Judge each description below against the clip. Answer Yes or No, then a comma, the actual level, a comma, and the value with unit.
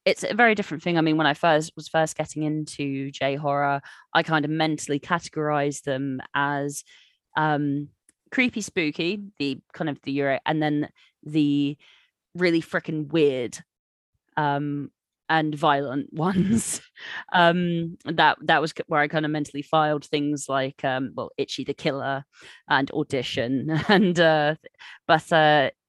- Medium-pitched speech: Yes, medium, 150 Hz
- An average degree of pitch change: No, narrow, 2.2 semitones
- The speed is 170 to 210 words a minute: No, average, 150 wpm